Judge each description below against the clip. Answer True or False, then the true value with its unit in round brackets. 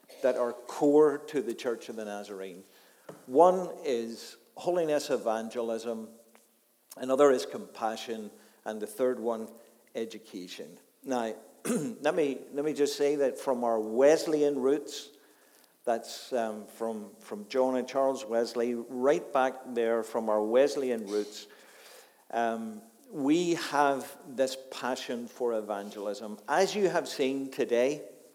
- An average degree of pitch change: True (3.3 semitones)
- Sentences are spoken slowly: True (125 wpm)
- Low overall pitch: True (120 Hz)